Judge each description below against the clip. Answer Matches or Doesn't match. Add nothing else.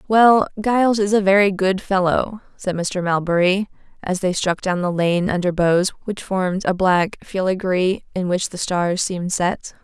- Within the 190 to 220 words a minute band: Doesn't match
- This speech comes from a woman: Matches